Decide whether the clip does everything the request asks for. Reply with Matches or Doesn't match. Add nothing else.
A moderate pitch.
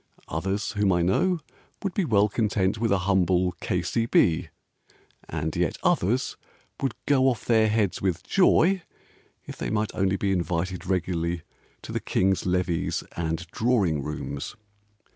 Doesn't match